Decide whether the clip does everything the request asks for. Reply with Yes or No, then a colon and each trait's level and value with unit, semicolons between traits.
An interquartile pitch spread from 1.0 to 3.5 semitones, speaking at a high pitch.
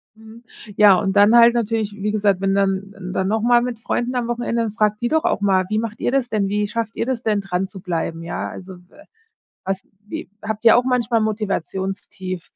Yes: average, 3.1 semitones; high, 210 Hz